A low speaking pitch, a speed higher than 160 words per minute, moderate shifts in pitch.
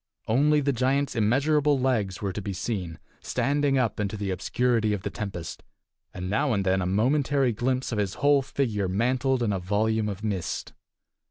Yes: low, 110 Hz; average, 180 wpm; average, 5.0 semitones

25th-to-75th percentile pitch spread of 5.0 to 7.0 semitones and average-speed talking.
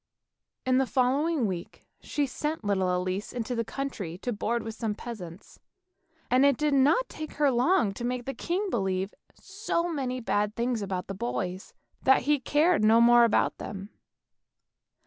Yes: wide, 5.6 semitones; average, 165 wpm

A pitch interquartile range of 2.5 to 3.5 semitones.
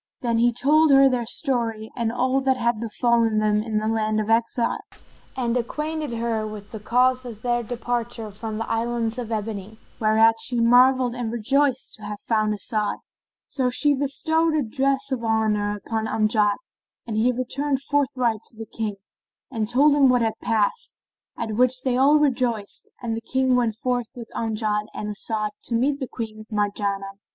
Yes: average, 2.9 semitones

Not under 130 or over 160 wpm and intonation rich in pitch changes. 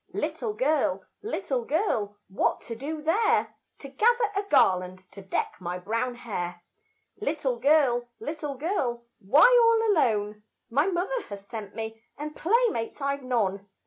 Yes: average, 145 wpm; wide, 8.5 semitones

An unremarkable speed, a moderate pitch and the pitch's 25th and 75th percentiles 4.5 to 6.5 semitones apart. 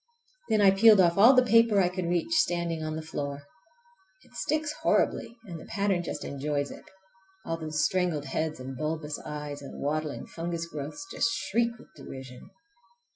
Yes: average, 175 wpm; medium, 165 Hz; average, 5.2 semitones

